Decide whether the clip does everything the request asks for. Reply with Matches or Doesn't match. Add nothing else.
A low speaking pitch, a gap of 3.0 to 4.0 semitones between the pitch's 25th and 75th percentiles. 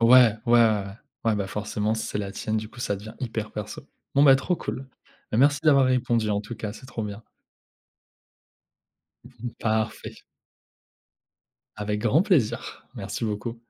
Matches